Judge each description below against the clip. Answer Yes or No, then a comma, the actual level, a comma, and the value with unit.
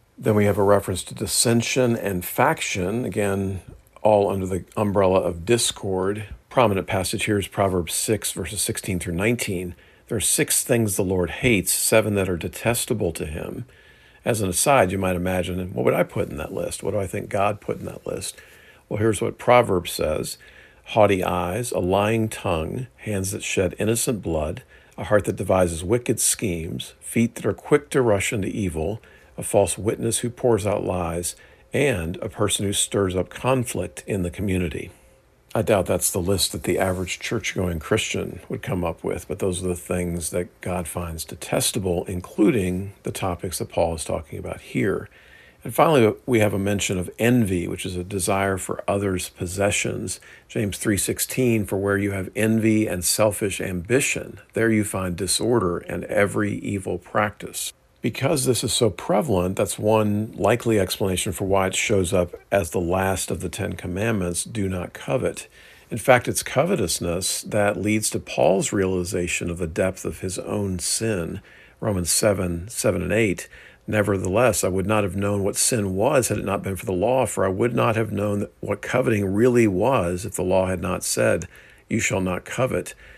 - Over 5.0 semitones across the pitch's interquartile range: No, average, 3.2 semitones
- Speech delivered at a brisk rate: No, average, 185 wpm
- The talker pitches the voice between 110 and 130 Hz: No, low, 100 Hz